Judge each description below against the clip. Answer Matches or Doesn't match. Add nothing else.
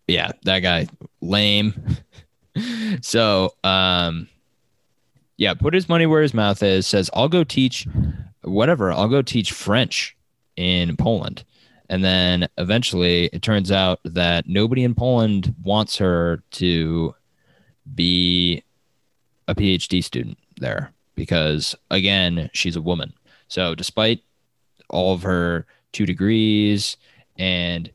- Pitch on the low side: Matches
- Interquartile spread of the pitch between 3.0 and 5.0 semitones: Matches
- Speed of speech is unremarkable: Doesn't match